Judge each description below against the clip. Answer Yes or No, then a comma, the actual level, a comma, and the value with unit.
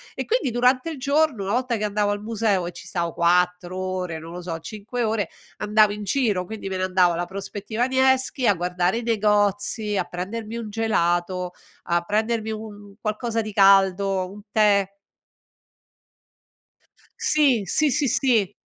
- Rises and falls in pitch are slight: No, average, 3.8 semitones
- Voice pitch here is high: Yes, high, 205 Hz